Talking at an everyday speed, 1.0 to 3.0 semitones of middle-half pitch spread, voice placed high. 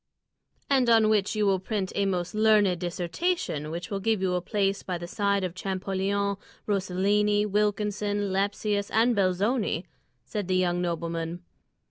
Yes: average, 150 wpm; narrow, 2.4 semitones; high, 195 Hz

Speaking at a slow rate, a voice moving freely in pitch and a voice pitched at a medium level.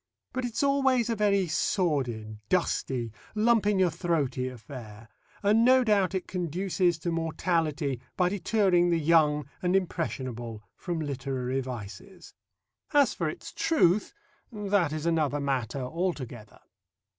Yes: slow, 130 wpm; wide, 6.6 semitones; medium, 170 Hz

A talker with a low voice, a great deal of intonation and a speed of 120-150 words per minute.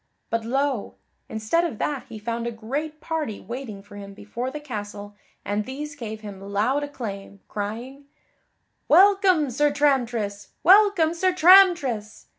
No: very high, 250 Hz; wide, 6.0 semitones; average, 140 wpm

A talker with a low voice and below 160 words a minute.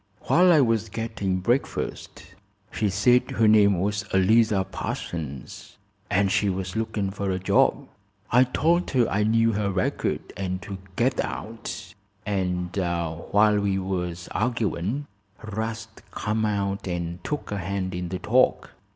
Yes: low, 100 Hz; average, 140 wpm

